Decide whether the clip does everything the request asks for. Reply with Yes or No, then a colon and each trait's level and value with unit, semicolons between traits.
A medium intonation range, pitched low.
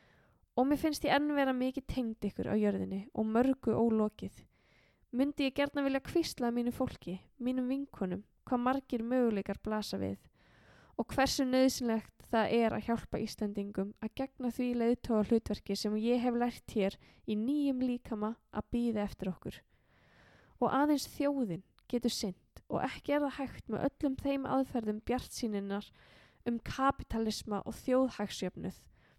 No: average, 3.8 semitones; high, 240 Hz